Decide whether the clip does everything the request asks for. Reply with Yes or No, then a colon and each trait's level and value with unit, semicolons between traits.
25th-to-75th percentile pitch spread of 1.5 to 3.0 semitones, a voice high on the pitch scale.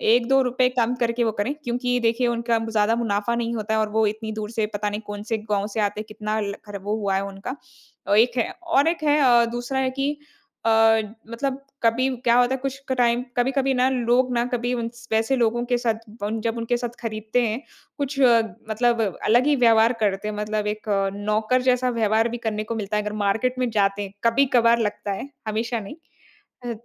Yes: narrow, 2.6 semitones; high, 230 Hz